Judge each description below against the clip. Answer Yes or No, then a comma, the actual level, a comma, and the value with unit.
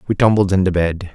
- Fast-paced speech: Yes, fast, 210 wpm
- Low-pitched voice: Yes, very low, 95 Hz